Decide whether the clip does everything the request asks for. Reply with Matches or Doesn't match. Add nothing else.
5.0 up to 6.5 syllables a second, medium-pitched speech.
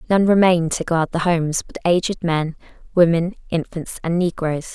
Matches